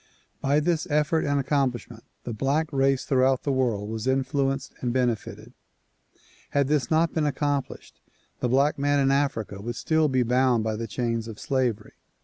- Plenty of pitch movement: No, average, 3.2 semitones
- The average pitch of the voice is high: No, low, 135 Hz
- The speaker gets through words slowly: No, average, 165 wpm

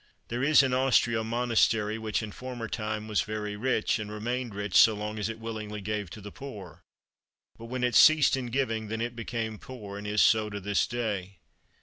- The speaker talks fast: Yes, fast, 210 wpm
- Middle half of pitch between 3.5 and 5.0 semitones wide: No, narrow, 2.4 semitones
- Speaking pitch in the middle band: No, low, 110 Hz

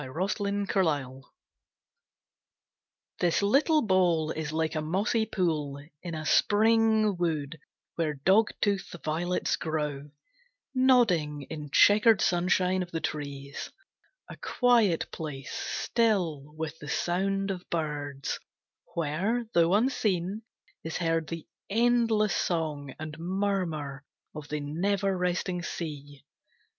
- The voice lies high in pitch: No, medium, 170 Hz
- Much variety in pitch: No, average, 4.8 semitones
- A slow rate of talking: Yes, slow, 110 wpm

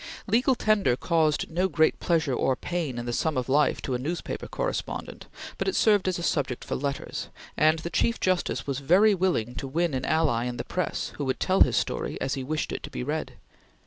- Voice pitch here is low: No, medium, 155 Hz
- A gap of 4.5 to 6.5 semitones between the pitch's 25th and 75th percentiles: Yes, wide, 5.6 semitones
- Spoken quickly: Yes, fast, 220 wpm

